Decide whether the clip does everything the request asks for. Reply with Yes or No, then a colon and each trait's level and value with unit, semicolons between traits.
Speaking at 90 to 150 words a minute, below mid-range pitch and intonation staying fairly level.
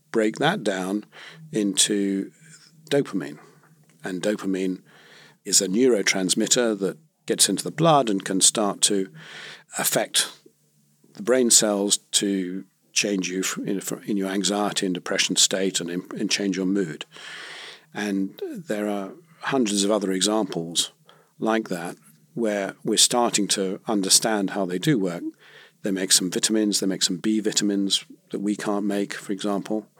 Yes: average, 140 wpm; low, 100 Hz; narrow, 2.3 semitones